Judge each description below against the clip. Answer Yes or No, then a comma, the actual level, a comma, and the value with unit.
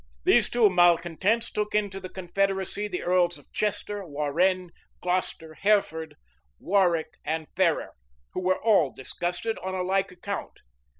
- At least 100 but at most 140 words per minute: Yes, slow, 135 wpm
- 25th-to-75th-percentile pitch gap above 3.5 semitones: No, narrow, 2.6 semitones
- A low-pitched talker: No, medium, 185 Hz